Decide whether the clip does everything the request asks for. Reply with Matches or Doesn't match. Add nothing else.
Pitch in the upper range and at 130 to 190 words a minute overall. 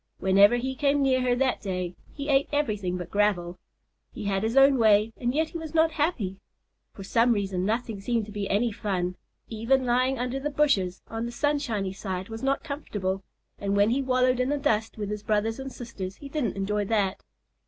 Doesn't match